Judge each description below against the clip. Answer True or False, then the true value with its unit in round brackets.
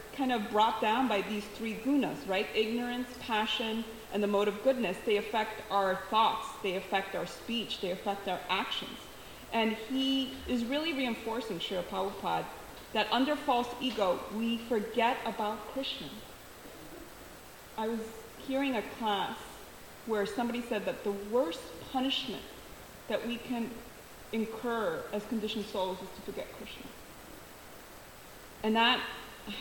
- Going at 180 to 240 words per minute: False (140 wpm)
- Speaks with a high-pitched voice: True (225 Hz)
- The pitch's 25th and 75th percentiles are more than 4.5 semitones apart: False (2.6 semitones)